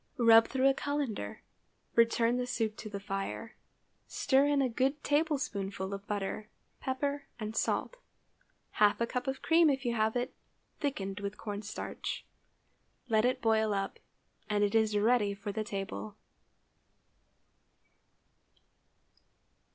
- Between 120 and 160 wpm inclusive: Yes, slow, 135 wpm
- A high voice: Yes, high, 225 Hz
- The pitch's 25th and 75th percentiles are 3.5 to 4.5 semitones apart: Yes, average, 4.2 semitones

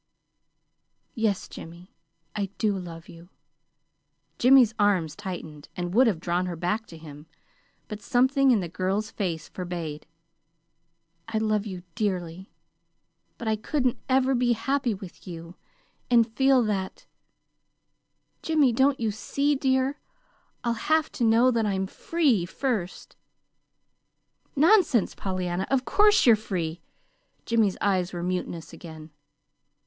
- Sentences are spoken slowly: Yes, slow, 125 wpm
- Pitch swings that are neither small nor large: No, wide, 5.9 semitones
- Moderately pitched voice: No, high, 210 Hz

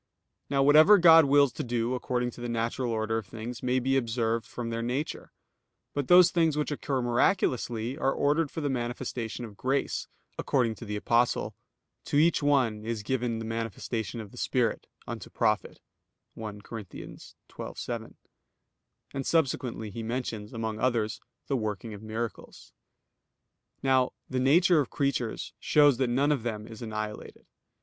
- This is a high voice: No, low, 120 Hz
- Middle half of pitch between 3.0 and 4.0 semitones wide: Yes, average, 3.4 semitones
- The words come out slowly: No, average, 155 wpm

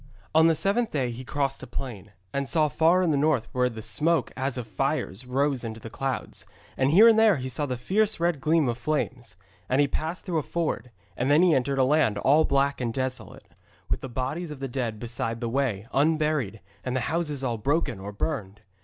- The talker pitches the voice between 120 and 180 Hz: Yes, low, 135 Hz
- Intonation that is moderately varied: Yes, average, 4.5 semitones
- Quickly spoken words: Yes, fast, 220 wpm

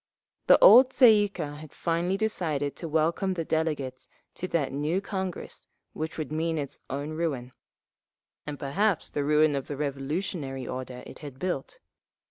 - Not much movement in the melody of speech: No, average, 4.1 semitones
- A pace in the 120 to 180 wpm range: Yes, average, 155 wpm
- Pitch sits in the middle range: Yes, medium, 155 Hz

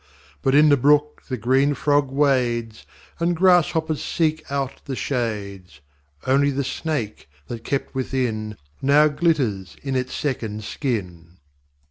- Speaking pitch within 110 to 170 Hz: Yes, low, 135 Hz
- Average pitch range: Yes, average, 4.6 semitones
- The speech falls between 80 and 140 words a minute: Yes, slow, 135 wpm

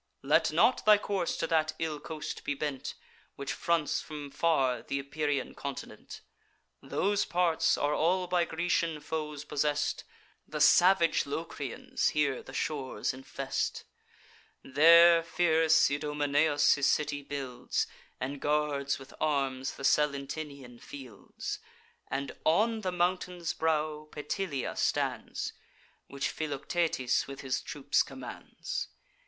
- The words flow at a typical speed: No, slow, 120 wpm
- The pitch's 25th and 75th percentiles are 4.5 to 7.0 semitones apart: No, average, 3.0 semitones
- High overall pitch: No, medium, 150 Hz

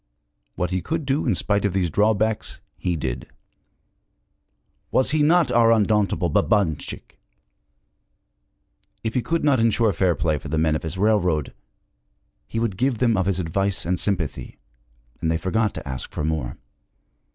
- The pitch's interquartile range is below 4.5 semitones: No, wide, 5.5 semitones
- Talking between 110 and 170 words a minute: Yes, average, 160 wpm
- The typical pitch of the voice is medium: No, low, 100 Hz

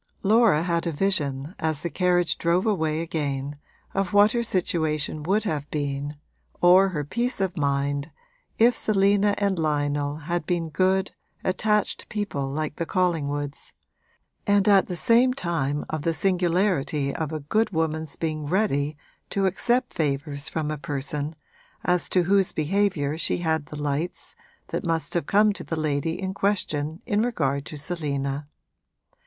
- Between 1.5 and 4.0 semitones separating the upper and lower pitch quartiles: No, average, 4.8 semitones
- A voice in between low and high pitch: Yes, medium, 165 Hz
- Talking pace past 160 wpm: No, average, 155 wpm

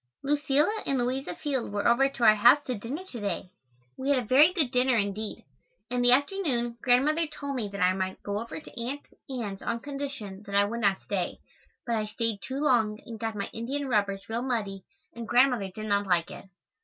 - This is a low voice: No, high, 235 Hz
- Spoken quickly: Yes, fast, 210 wpm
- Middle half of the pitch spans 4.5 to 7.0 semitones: Yes, average, 4.8 semitones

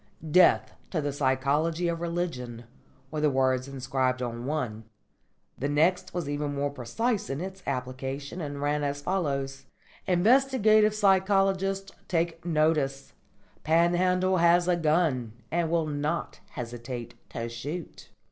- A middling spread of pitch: Yes, average, 4.8 semitones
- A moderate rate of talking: No, slow, 130 wpm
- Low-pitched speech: No, medium, 155 Hz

